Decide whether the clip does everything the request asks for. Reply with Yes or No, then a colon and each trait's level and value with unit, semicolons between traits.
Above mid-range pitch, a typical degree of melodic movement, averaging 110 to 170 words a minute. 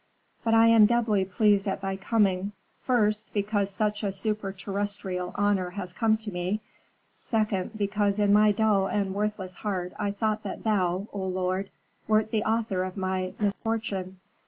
No: high, 205 Hz; narrow, 2.1 semitones; average, 160 wpm